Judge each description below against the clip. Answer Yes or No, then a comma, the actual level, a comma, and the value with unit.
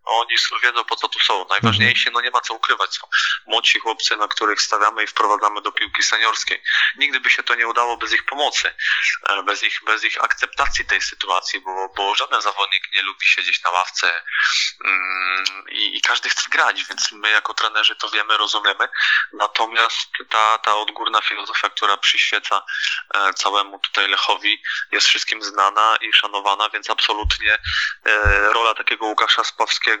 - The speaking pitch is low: Yes, low, 115 Hz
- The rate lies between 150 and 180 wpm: Yes, fast, 160 wpm